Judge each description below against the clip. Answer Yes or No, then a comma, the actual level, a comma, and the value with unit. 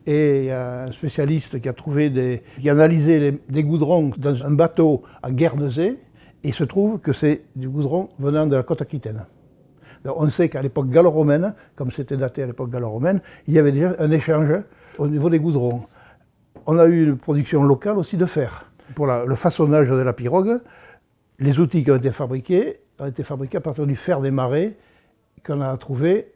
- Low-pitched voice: No, medium, 150 Hz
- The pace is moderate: Yes, average, 195 wpm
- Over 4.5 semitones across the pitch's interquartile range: No, average, 3.3 semitones